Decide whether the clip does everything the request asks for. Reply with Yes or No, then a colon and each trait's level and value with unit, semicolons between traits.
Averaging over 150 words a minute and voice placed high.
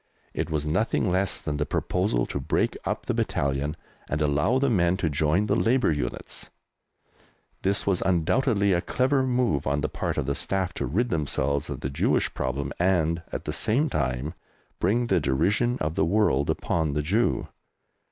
No: average, 175 wpm; very low, 85 Hz